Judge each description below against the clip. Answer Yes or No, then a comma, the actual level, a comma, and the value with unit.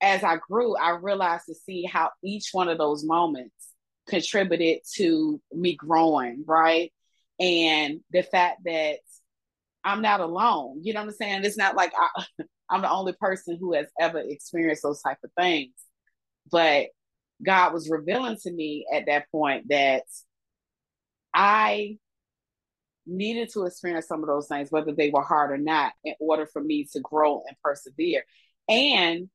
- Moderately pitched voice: Yes, medium, 170 Hz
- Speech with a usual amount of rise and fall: Yes, average, 4.1 semitones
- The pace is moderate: Yes, average, 160 wpm